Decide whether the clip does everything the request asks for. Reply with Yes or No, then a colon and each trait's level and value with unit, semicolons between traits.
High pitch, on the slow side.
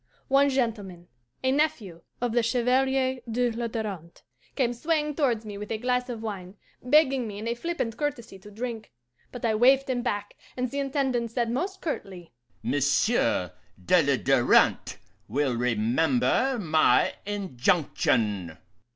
No: high, 230 Hz; average, 145 wpm